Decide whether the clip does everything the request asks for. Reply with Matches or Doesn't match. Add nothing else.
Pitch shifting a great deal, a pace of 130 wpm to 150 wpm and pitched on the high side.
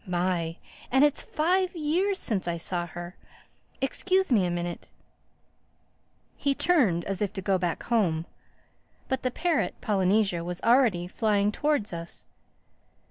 Matches